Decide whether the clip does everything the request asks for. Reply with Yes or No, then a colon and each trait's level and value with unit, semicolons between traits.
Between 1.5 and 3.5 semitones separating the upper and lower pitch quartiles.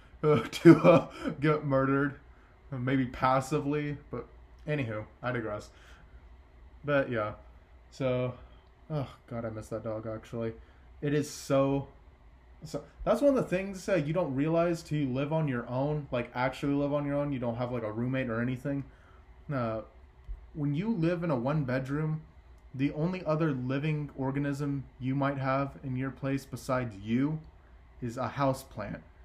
No: average, 4.9 semitones